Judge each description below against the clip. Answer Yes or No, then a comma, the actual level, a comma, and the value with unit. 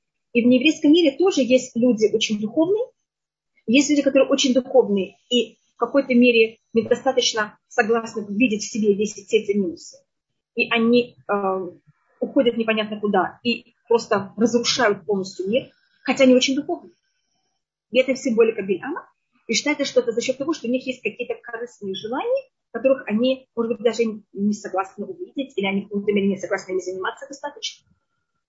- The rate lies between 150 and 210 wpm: Yes, fast, 160 wpm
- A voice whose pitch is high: Yes, high, 235 Hz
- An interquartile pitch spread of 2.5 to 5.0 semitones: Yes, average, 4.0 semitones